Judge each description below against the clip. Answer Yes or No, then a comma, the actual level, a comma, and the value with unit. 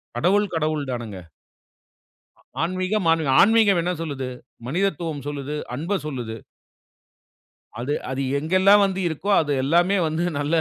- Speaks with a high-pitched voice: No, medium, 160 Hz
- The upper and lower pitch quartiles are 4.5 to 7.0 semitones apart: Yes, average, 4.8 semitones